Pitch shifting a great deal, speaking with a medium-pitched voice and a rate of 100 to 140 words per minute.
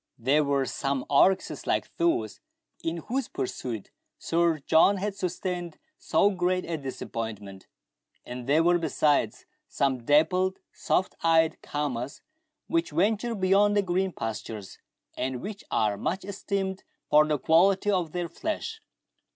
Yes: wide, 5.7 semitones; medium, 170 Hz; slow, 135 wpm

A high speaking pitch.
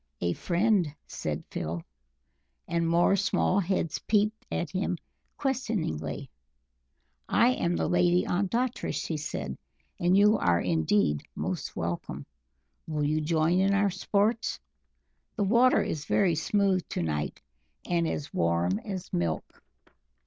No: medium, 175 Hz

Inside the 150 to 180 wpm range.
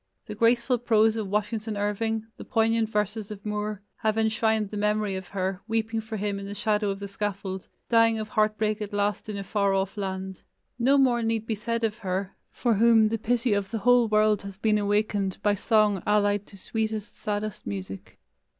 No: average, 200 wpm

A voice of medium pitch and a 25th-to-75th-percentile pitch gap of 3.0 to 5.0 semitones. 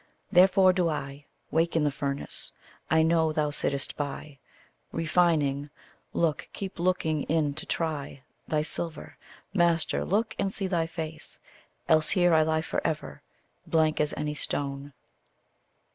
No: medium, 160 Hz; narrow, 2.5 semitones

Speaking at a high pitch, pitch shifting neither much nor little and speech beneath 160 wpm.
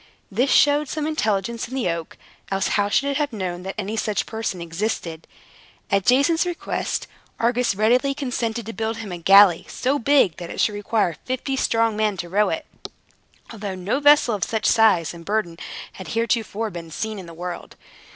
No: high, 220 Hz; average, 4.9 semitones; average, 190 wpm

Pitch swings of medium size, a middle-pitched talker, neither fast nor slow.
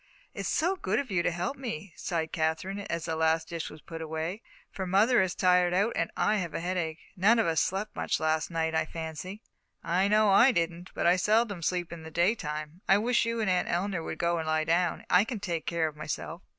No: average, 3.8 semitones; medium, 175 Hz; fast, 230 wpm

